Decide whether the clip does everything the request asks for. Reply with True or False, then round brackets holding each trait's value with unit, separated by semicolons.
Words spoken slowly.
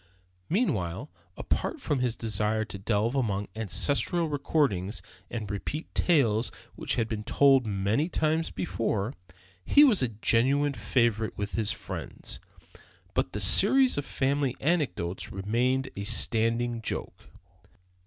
True (125 wpm)